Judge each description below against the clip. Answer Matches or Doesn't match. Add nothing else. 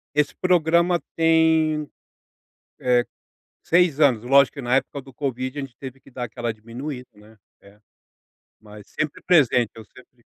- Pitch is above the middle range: Doesn't match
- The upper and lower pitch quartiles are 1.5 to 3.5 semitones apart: Doesn't match